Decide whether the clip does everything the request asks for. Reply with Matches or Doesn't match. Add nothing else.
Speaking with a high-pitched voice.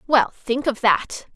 Matches